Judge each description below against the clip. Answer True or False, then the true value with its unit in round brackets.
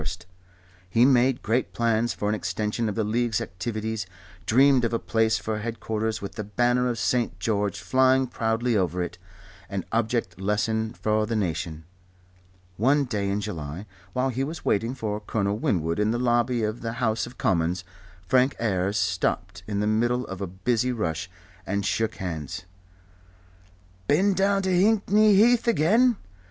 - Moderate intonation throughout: True (3.7 semitones)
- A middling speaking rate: True (160 wpm)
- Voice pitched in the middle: False (110 Hz)